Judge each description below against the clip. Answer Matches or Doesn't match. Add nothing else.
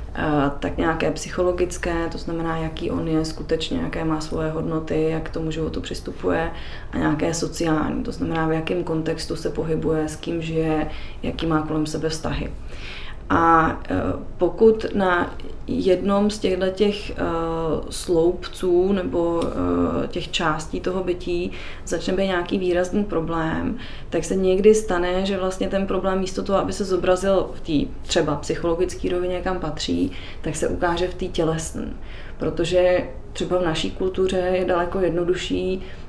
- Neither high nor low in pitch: Matches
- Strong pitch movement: Doesn't match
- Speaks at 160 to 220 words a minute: Doesn't match